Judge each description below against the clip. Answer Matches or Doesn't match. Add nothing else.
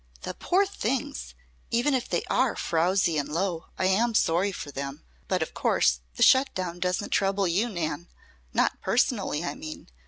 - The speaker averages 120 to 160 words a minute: Doesn't match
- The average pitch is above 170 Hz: Matches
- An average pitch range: Doesn't match